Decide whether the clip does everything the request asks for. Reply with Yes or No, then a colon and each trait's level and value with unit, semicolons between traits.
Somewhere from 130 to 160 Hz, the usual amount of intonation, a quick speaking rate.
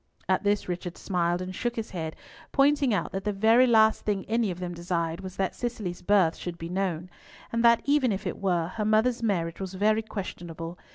No: high, 195 Hz; average, 3.9 semitones; fast, 210 wpm